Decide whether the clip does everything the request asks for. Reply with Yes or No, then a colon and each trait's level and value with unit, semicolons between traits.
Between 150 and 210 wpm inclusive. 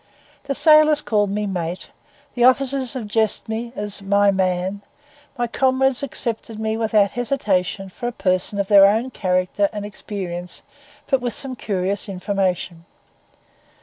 No: average, 140 wpm